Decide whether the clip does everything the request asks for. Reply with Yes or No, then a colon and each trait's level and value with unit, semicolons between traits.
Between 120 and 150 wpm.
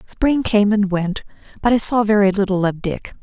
No: fast, 205 wpm